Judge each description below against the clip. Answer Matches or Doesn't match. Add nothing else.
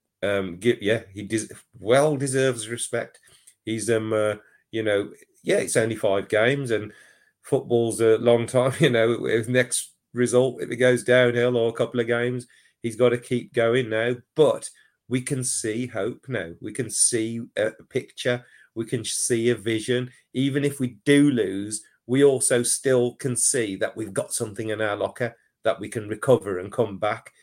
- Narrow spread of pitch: Matches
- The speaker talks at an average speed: Matches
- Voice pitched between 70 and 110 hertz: Doesn't match